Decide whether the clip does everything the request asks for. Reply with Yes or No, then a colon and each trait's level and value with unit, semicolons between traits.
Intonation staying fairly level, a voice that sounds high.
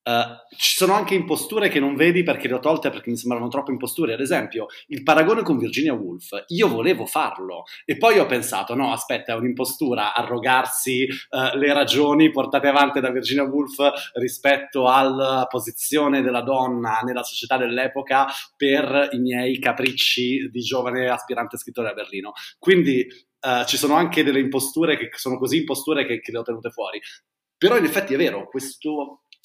No: narrow, 2.2 semitones; low, 135 Hz